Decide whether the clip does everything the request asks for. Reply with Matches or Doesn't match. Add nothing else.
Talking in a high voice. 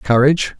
Doesn't match